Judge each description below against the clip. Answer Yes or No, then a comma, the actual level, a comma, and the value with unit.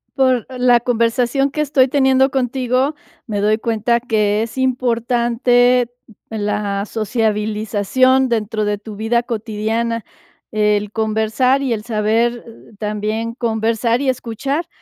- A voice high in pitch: Yes, high, 230 Hz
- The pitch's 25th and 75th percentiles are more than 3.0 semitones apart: No, average, 2.7 semitones